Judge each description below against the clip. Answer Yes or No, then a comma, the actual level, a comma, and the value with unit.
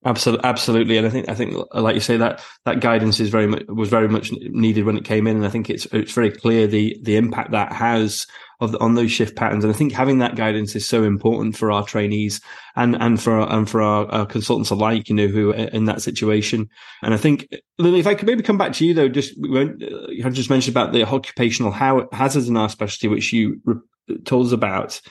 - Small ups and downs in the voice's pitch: Yes, narrow, 2.2 semitones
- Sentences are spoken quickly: Yes, fast, 235 wpm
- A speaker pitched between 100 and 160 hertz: Yes, low, 115 Hz